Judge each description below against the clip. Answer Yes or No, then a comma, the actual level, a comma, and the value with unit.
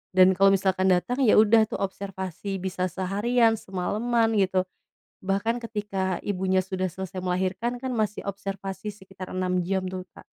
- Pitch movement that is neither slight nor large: No, narrow, 2.1 semitones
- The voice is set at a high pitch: Yes, high, 195 Hz